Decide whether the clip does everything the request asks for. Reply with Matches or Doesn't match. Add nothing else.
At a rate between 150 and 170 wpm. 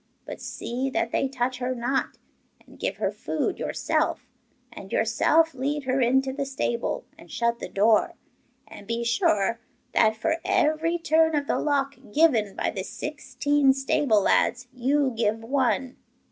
Matches